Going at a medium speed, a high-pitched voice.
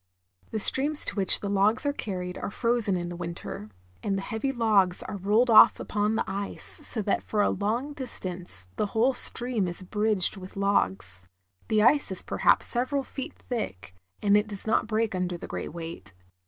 Yes: average, 190 wpm; high, 205 Hz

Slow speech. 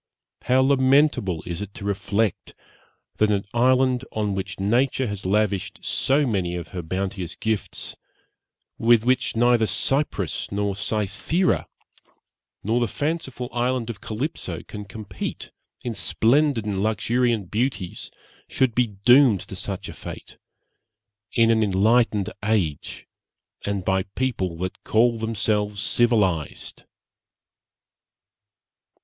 Yes: slow, 120 wpm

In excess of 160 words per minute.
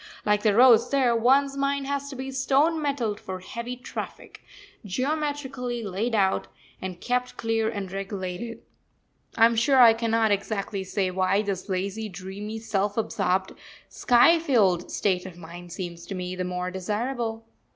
No: average, 155 wpm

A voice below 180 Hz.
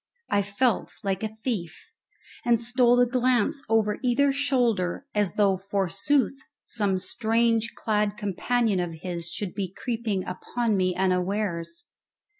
No: high, 210 Hz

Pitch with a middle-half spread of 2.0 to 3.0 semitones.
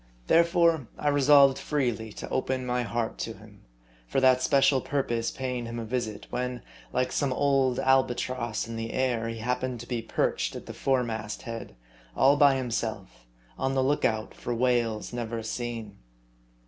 Yes: narrow, 2.6 semitones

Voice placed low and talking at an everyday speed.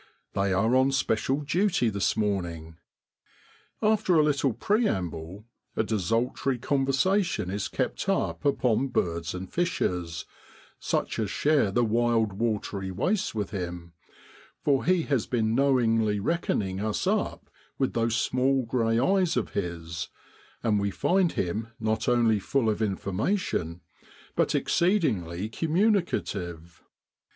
No: low, 115 Hz; slow, 125 wpm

